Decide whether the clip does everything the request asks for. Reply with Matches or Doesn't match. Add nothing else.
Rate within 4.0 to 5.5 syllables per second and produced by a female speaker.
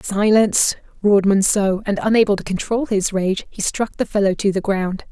Matches